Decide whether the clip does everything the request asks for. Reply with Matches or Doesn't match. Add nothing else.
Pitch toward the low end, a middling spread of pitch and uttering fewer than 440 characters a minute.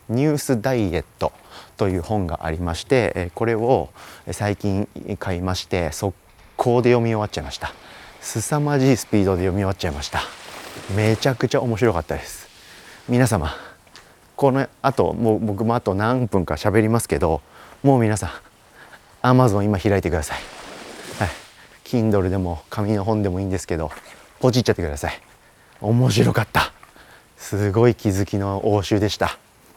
Matches